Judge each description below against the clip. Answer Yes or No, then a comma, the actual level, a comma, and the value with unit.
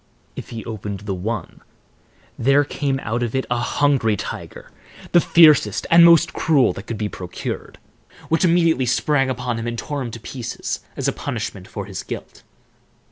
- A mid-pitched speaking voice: No, low, 125 Hz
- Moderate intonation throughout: Yes, average, 4.6 semitones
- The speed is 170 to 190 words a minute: Yes, average, 175 wpm